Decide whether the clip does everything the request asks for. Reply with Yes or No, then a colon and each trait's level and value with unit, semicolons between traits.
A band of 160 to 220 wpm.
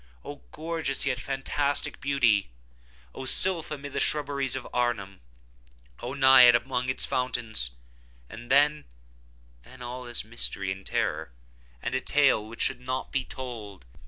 No: slow, 135 wpm